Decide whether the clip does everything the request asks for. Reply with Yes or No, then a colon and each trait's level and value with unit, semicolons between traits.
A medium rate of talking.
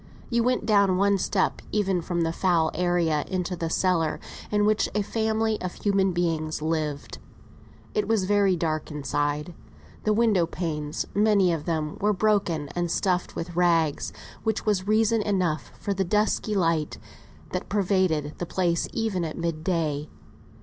Yes: average, 155 wpm